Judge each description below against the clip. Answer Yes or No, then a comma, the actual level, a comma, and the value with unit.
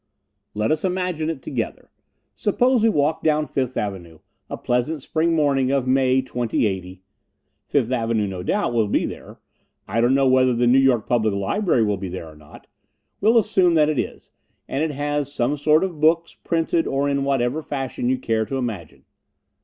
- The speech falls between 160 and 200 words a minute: Yes, average, 185 wpm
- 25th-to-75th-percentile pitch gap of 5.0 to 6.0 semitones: Yes, average, 5.3 semitones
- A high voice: No, low, 135 Hz